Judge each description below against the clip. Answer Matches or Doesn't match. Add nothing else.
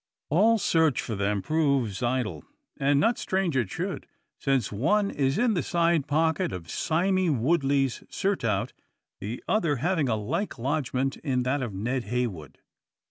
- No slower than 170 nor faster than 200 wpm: Doesn't match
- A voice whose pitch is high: Doesn't match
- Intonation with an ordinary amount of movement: Doesn't match